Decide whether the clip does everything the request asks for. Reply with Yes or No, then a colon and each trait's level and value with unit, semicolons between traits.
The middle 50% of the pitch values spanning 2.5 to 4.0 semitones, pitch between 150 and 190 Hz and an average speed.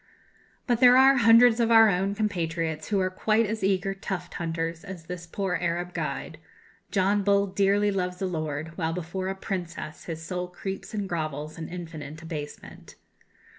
Yes: average, 3.5 semitones; medium, 185 Hz; average, 170 wpm